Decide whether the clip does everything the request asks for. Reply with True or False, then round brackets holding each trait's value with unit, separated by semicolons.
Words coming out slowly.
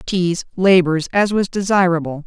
True (130 wpm)